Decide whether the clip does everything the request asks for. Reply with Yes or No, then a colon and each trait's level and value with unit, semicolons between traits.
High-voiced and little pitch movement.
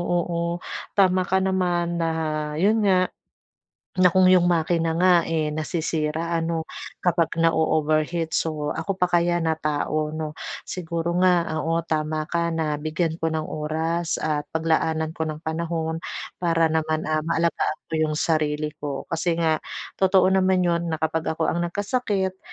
No: medium, 165 Hz; narrow, 1.8 semitones